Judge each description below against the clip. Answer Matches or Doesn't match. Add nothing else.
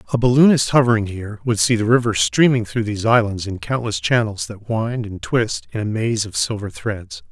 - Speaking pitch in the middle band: Doesn't match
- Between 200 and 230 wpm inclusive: Matches